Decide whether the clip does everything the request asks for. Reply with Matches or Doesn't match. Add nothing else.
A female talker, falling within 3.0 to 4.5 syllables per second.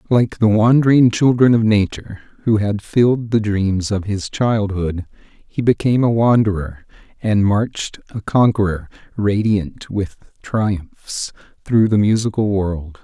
Doesn't match